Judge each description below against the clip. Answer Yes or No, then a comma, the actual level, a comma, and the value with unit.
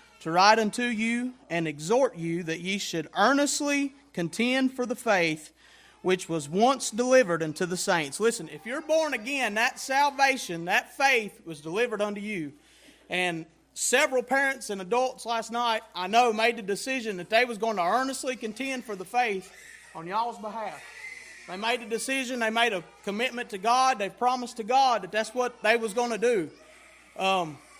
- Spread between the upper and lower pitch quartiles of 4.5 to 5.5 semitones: Yes, average, 5.2 semitones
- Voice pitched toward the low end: No, high, 230 Hz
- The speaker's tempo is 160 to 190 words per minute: Yes, average, 180 wpm